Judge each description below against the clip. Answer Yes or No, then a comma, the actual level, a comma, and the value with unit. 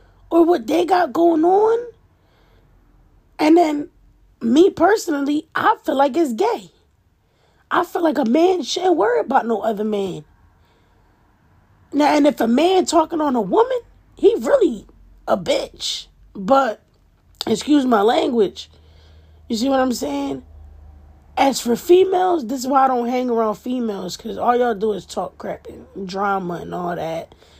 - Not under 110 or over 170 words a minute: Yes, average, 155 wpm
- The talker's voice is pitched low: No, very high, 260 Hz